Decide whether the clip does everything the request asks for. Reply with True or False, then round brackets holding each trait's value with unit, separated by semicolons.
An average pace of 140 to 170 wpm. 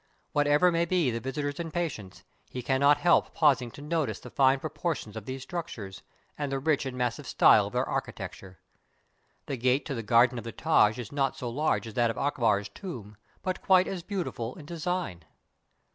False (190 wpm)